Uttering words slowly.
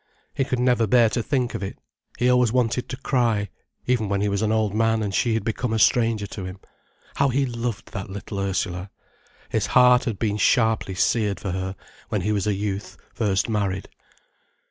No: average, 195 wpm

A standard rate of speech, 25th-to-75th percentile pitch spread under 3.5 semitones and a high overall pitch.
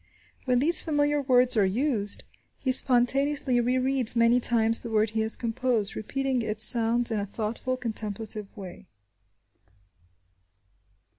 No: slow, 130 wpm; average, 2.8 semitones; high, 240 Hz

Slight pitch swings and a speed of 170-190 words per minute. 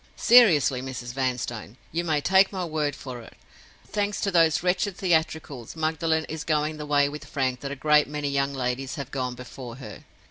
No: average, 3.6 semitones; average, 180 wpm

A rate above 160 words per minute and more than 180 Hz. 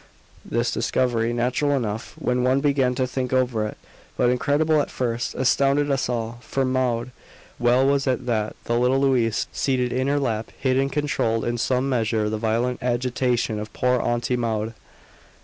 No: average, 170 wpm; low, 125 Hz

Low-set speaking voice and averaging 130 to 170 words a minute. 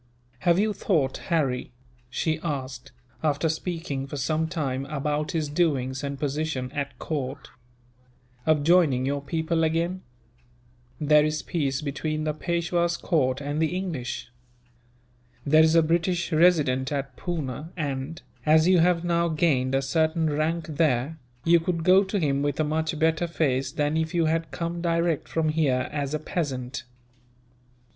No: medium, 155 Hz; average, 150 wpm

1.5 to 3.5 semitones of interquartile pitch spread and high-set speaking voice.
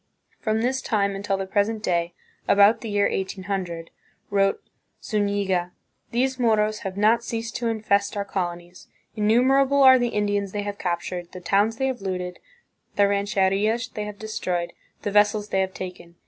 Yes: narrow, 2.5 semitones; high, 205 Hz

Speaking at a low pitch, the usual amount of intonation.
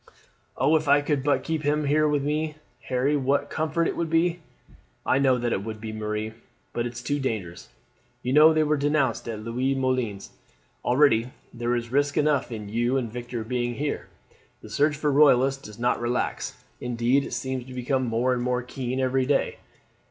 Yes: low, 130 Hz; average, 3.4 semitones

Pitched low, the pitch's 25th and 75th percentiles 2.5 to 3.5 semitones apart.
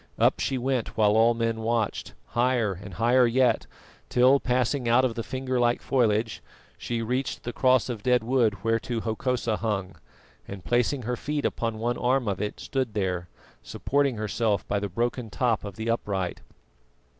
Yes: low, 115 Hz; average, 2.8 semitones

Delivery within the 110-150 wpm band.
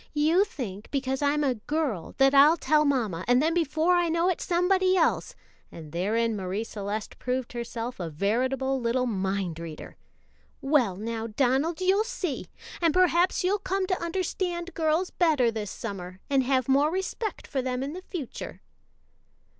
No: average, 160 wpm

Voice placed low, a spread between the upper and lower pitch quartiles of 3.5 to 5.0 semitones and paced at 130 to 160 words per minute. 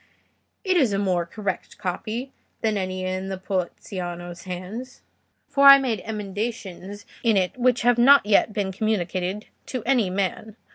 No: high, 205 Hz; average, 3.9 semitones; average, 145 wpm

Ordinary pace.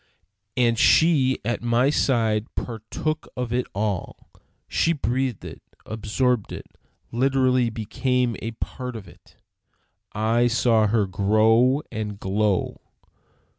No: slow, 115 wpm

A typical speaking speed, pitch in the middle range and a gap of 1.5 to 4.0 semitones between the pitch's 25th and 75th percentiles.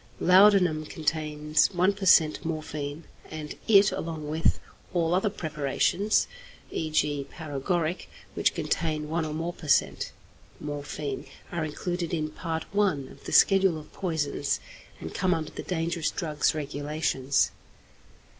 No: slow, 130 wpm; medium, 155 Hz; narrow, 2.6 semitones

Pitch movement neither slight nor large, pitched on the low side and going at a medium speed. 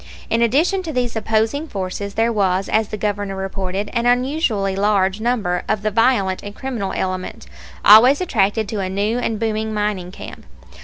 No: average, 3.2 semitones; high, 215 Hz; average, 170 wpm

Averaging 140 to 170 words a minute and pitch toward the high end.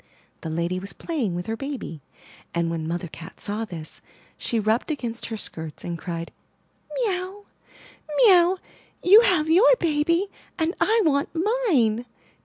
Yes: average, 155 wpm; very high, 255 Hz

